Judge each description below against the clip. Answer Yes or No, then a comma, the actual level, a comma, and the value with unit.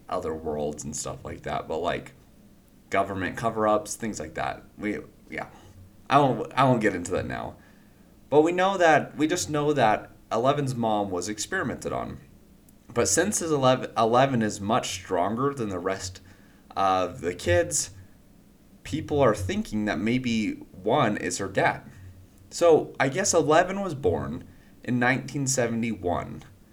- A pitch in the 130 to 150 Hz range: No, low, 110 Hz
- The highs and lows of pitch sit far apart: Yes, wide, 6.0 semitones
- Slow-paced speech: No, average, 150 wpm